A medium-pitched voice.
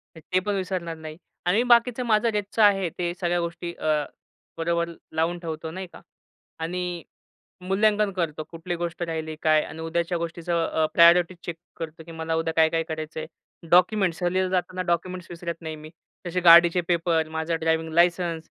Yes: medium, 170 Hz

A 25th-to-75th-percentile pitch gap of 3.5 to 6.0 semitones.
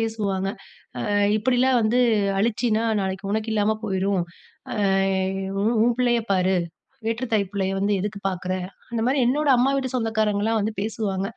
No: average, 3.1 semitones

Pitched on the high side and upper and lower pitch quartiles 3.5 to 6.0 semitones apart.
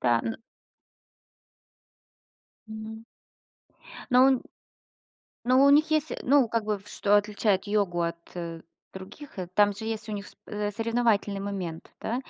No: high, 210 Hz; average, 2.7 semitones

